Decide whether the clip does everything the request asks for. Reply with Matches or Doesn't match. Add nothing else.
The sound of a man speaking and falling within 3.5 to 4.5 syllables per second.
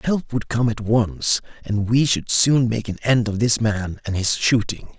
Matches